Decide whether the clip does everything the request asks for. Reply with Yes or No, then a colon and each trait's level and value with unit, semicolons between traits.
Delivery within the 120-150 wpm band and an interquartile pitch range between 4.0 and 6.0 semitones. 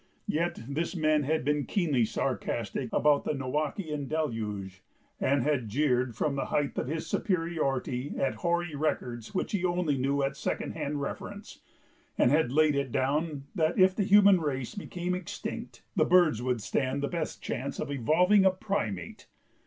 No: average, 165 wpm; average, 4.5 semitones